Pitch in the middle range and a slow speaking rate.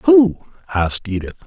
Yes: medium, 145 Hz; slow, 125 wpm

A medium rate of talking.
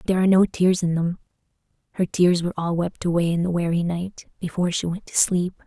No: fast, 235 wpm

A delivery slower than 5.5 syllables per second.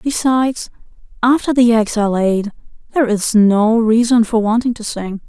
Yes: 5.0 syllables/s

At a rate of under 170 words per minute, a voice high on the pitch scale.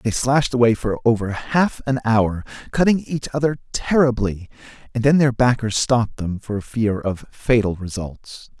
No: average, 160 wpm; low, 120 Hz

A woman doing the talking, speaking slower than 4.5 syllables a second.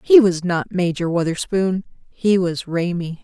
Yes: female; 4.2 syllables/s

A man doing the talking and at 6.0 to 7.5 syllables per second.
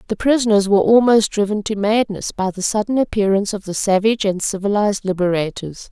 No: female; 6.1 syllables/s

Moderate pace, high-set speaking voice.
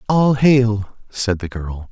No: average, 155 wpm; low, 110 Hz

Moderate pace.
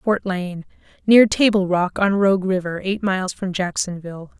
Yes: average, 150 wpm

